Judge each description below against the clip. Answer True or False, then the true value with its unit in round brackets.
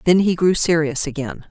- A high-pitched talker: False (165 Hz)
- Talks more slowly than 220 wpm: True (200 wpm)